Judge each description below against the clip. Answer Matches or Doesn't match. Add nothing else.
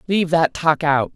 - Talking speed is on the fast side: Matches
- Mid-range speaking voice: Matches